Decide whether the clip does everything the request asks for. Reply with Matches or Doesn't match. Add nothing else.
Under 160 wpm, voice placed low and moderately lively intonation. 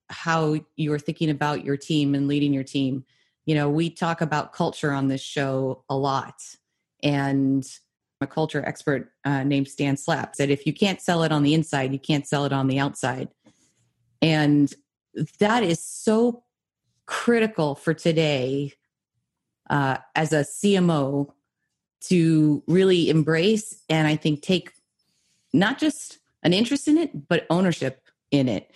Doesn't match